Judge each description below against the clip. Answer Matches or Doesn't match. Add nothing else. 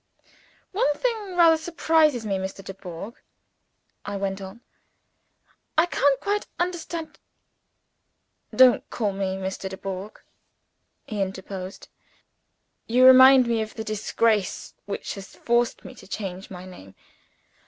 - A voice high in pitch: Matches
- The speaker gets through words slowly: Matches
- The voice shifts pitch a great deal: Matches